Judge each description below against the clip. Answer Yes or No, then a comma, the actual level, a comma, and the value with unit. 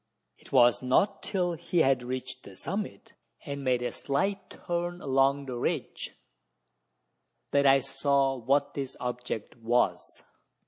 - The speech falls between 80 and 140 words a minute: Yes, slow, 135 wpm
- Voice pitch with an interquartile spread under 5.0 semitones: Yes, average, 2.9 semitones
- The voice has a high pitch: No, low, 135 Hz